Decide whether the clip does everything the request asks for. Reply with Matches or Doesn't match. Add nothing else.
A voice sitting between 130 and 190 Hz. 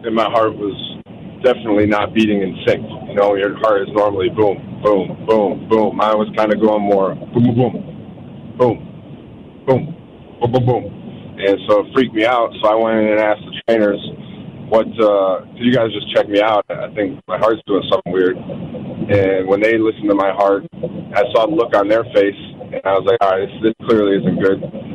Doesn't match